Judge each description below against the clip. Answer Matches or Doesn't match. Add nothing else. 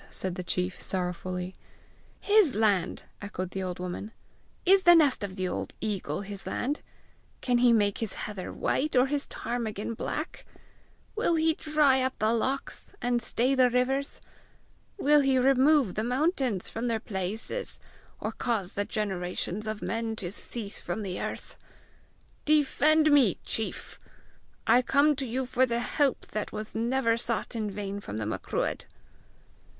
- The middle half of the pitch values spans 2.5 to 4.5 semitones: Doesn't match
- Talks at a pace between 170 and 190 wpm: Doesn't match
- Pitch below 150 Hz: Doesn't match